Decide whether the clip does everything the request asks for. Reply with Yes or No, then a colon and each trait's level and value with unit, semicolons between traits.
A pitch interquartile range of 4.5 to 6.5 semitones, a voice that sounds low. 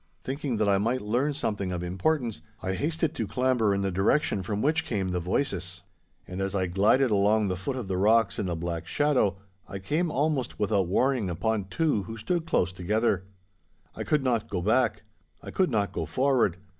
Yes: wide, 5.5 semitones; low, 105 Hz